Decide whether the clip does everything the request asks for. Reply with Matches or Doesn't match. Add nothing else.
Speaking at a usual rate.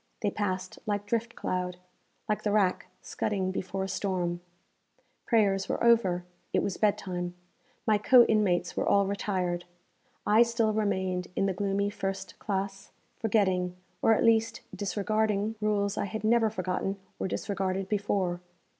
Matches